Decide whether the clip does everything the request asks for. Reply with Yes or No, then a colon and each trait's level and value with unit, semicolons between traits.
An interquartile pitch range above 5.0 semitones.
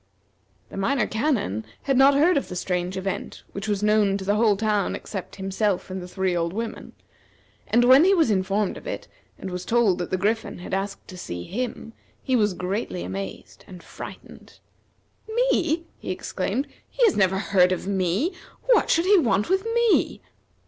Yes: wide, 5.4 semitones